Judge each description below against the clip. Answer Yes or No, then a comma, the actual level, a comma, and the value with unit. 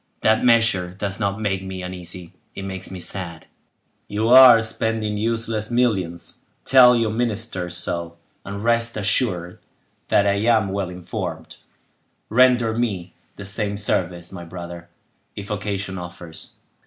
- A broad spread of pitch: No, average, 3.9 semitones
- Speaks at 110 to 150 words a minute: Yes, slow, 135 wpm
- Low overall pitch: Yes, low, 100 Hz